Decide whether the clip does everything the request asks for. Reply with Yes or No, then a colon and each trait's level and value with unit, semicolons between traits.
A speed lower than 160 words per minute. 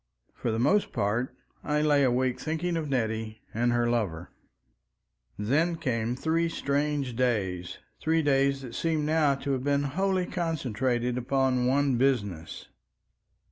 Yes: slow, 135 wpm